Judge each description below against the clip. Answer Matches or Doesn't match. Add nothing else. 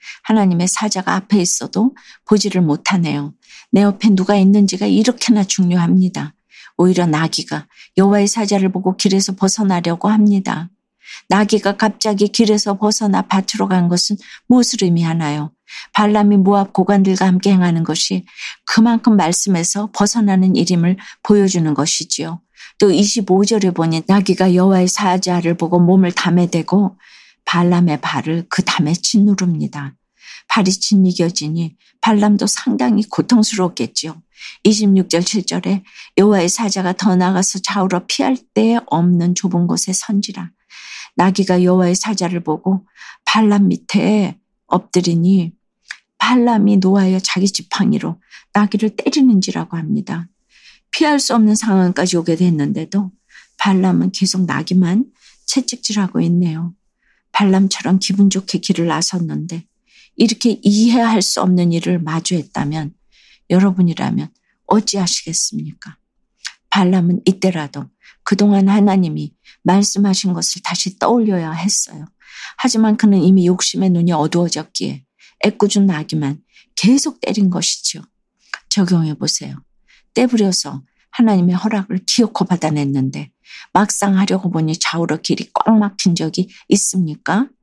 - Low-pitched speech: Doesn't match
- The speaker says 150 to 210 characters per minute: Doesn't match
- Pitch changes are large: Doesn't match